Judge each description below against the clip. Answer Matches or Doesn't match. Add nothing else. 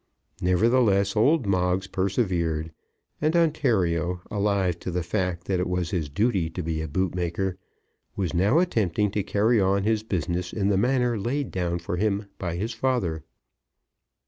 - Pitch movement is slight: Doesn't match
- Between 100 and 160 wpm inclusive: Matches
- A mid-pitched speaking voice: Doesn't match